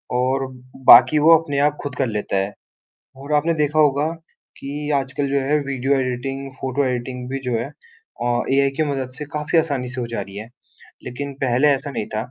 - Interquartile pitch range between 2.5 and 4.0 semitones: Yes, average, 2.8 semitones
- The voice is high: No, low, 135 Hz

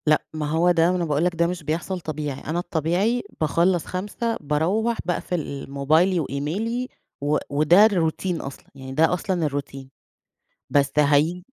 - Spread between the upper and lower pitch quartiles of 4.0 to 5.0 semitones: No, average, 3.5 semitones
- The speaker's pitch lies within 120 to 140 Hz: No, medium, 165 Hz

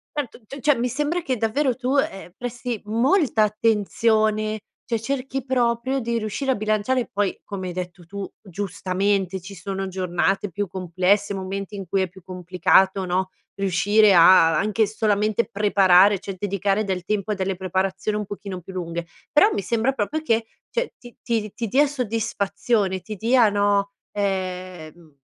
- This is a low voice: No, high, 205 Hz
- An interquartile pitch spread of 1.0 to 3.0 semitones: No, average, 3.4 semitones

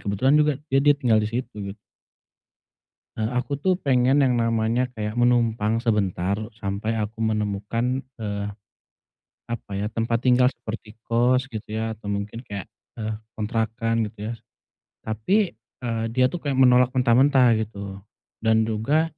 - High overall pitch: No, low, 115 Hz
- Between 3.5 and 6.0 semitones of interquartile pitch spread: No, average, 2.8 semitones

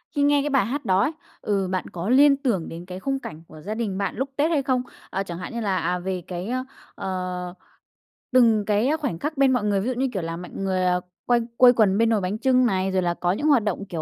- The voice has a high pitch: Yes, high, 205 Hz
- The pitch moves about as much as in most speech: No, wide, 5.8 semitones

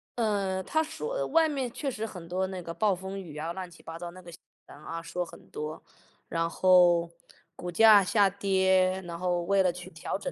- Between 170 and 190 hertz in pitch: Yes, medium, 185 Hz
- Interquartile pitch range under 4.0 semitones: Yes, average, 2.8 semitones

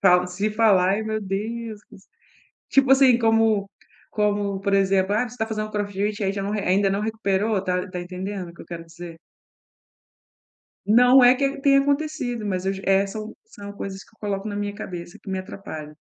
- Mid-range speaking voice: No, high, 205 Hz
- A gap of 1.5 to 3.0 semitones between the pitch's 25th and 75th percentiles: Yes, narrow, 2.5 semitones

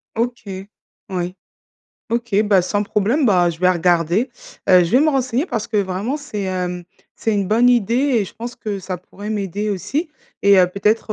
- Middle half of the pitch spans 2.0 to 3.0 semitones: No, average, 4.4 semitones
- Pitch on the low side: No, high, 205 Hz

